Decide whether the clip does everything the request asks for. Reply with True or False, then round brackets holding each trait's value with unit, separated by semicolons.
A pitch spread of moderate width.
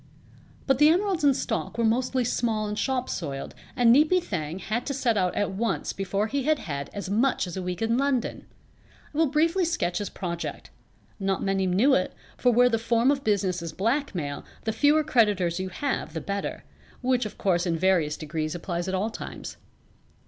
False (6.1 semitones)